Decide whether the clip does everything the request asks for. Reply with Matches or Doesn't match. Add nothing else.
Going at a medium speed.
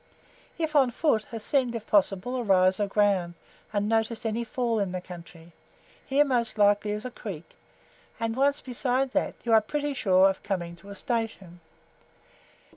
Matches